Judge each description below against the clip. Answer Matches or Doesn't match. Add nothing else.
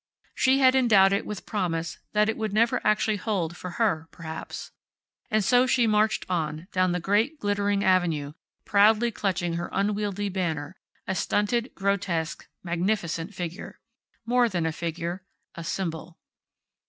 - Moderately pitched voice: Doesn't match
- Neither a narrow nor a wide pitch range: Matches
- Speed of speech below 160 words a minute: Matches